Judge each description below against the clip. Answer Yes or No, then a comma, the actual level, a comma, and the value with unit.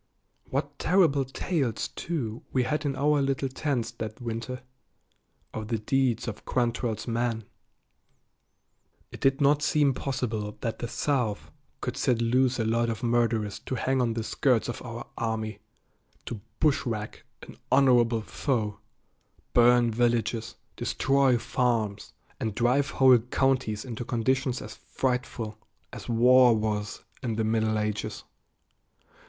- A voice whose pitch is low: Yes, low, 120 Hz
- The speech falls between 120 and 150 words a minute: Yes, slow, 135 wpm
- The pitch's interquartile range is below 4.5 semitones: Yes, average, 2.9 semitones